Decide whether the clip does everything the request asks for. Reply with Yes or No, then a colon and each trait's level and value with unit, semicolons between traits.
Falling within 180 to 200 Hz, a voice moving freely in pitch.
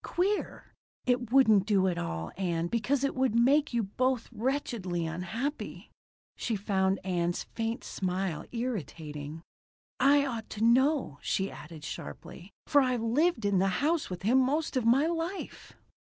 No: high, 225 Hz; wide, 6.4 semitones